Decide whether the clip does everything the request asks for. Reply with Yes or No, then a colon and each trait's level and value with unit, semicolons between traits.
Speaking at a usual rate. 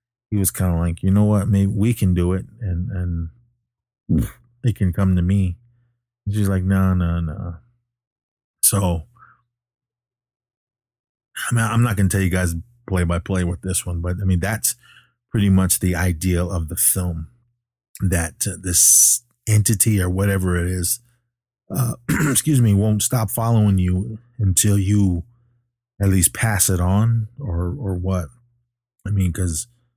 Yes: average, 160 wpm